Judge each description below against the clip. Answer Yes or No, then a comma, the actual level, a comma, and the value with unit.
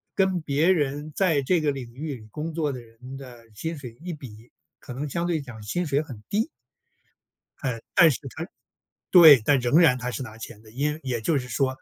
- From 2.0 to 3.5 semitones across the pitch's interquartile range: No, average, 4.5 semitones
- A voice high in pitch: No, medium, 140 Hz